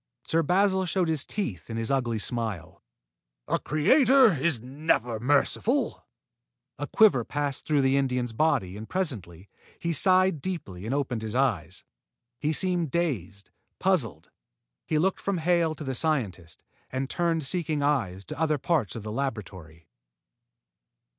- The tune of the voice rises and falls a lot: Yes, wide, 7.2 semitones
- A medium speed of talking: Yes, average, 145 wpm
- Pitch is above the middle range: No, medium, 140 Hz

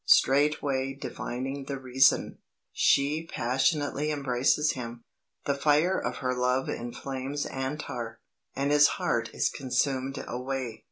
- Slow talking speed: Yes, slow, 115 wpm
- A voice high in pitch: No, low, 135 Hz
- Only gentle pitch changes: Yes, narrow, 2.2 semitones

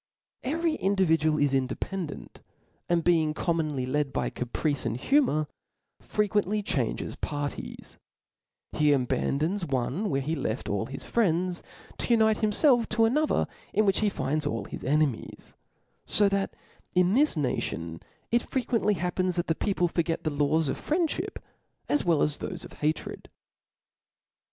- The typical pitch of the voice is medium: Yes, medium, 165 Hz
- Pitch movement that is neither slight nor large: No, wide, 6.3 semitones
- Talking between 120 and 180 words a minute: Yes, average, 145 wpm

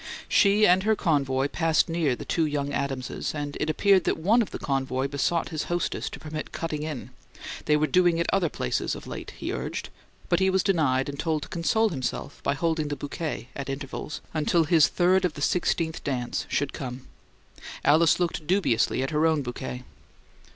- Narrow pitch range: No, average, 3.7 semitones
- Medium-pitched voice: Yes, medium, 155 Hz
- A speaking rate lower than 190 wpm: No, average, 195 wpm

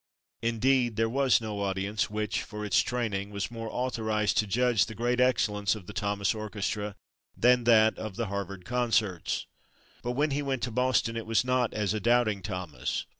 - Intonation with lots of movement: No, average, 3.0 semitones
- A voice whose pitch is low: Yes, low, 110 Hz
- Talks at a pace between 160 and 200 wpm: Yes, average, 180 wpm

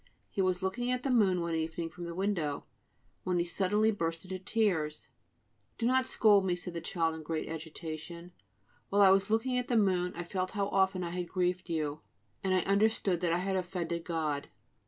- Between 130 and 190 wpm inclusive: No, average, 200 wpm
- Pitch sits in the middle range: Yes, medium, 180 Hz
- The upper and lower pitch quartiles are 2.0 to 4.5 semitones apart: Yes, average, 2.9 semitones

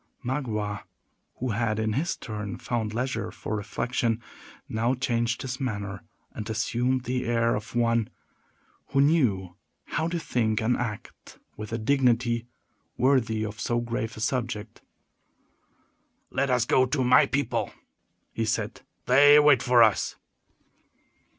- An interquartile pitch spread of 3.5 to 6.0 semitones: No, average, 2.8 semitones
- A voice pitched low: Yes, low, 120 Hz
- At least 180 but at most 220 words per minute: No, slow, 135 wpm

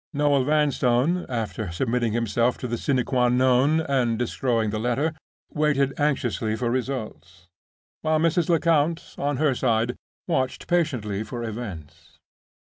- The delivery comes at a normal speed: No, slow, 130 wpm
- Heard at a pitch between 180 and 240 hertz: No, low, 125 Hz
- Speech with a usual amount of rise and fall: Yes, average, 4.2 semitones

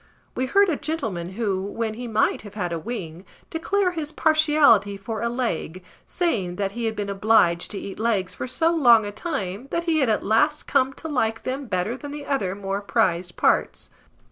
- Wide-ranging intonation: Yes, wide, 6.5 semitones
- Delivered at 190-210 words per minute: Yes, average, 200 wpm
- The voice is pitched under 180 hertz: No, high, 225 Hz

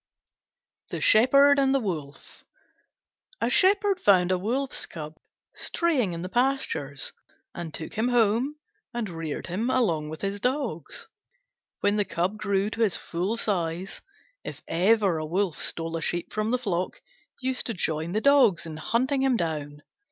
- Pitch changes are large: Yes, wide, 6.9 semitones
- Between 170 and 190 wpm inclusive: No, average, 160 wpm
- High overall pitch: Yes, high, 200 Hz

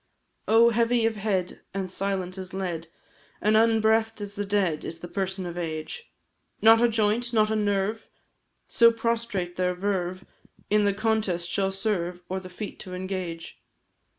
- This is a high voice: Yes, high, 200 Hz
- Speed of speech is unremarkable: Yes, average, 160 wpm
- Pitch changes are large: No, average, 3.3 semitones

